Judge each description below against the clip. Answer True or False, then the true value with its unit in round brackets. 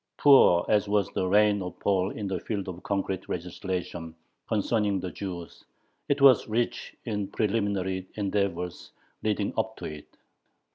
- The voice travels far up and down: False (2.5 semitones)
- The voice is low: True (100 Hz)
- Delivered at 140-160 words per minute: True (145 wpm)